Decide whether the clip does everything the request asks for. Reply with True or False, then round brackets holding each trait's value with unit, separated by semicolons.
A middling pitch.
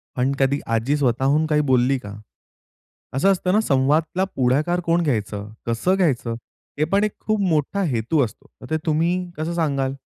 True (150 Hz)